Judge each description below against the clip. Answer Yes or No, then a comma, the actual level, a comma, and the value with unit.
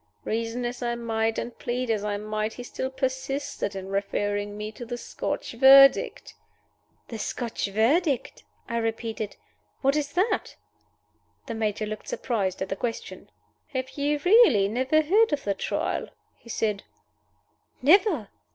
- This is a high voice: Yes, high, 235 Hz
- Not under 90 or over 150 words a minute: Yes, average, 145 wpm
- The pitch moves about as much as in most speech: Yes, average, 4.1 semitones